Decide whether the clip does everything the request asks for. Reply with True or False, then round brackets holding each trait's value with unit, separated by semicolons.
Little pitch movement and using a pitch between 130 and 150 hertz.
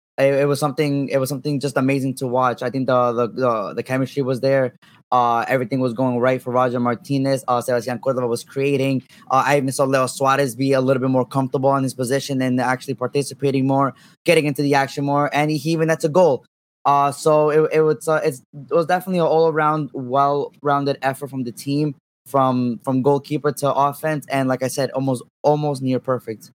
True (1.8 semitones; 135 Hz)